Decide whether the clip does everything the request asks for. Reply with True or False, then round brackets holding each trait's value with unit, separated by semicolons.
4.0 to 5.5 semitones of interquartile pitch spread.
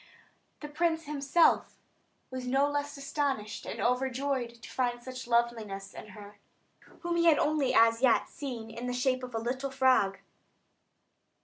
False (3.3 semitones)